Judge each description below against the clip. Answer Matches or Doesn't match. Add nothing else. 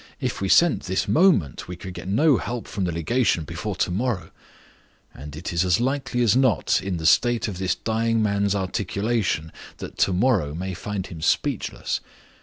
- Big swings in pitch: Doesn't match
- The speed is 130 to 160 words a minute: Doesn't match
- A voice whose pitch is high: Doesn't match